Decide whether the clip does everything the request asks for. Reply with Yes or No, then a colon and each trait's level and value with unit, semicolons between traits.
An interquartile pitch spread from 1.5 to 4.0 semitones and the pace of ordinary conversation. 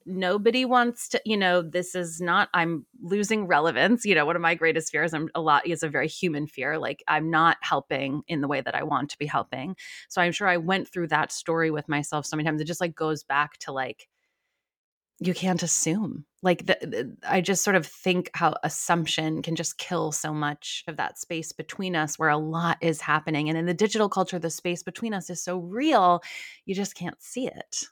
No: average, 3.1 semitones; fast, 225 wpm